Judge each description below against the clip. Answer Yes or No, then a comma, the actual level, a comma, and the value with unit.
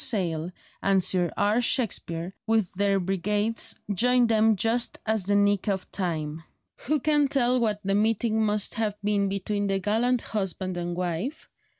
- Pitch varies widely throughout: No, average, 3.2 semitones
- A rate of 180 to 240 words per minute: No, average, 160 wpm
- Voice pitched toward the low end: No, high, 205 Hz